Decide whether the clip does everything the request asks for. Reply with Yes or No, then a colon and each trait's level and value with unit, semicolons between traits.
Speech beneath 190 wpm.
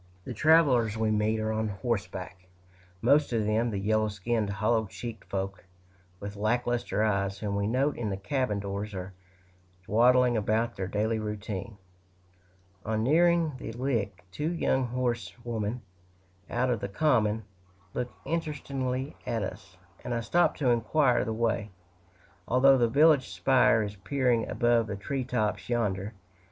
Yes: average, 150 wpm